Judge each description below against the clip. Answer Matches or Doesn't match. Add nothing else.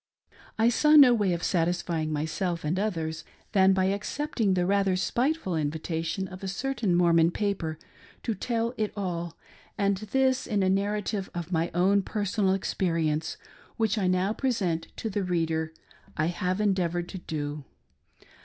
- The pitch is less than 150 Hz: Doesn't match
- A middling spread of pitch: Matches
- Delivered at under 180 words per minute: Matches